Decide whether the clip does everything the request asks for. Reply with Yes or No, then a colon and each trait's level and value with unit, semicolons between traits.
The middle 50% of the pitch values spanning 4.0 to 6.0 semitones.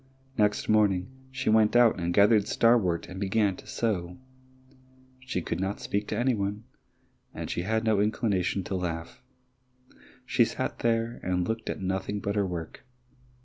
No: average, 3.3 semitones